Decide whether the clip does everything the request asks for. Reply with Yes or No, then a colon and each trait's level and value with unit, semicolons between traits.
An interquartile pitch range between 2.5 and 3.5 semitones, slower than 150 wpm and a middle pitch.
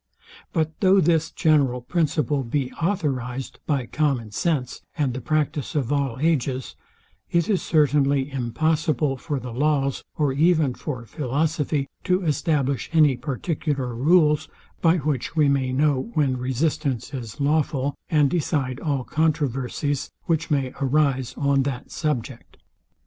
Yes: average, 3.1 semitones; slow, 135 wpm; medium, 145 Hz